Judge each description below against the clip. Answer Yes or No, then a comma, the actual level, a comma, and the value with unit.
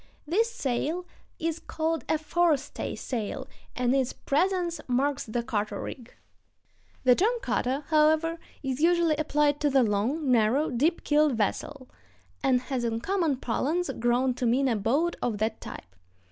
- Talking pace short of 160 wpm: Yes, average, 150 wpm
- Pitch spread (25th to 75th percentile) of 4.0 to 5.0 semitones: Yes, average, 4.7 semitones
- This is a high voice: Yes, very high, 275 Hz